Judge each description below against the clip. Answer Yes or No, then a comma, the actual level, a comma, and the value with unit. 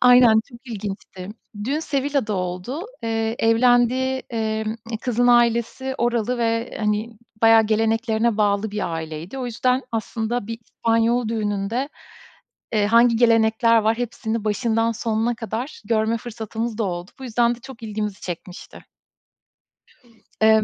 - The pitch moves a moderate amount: No, narrow, 1.8 semitones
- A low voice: No, high, 225 Hz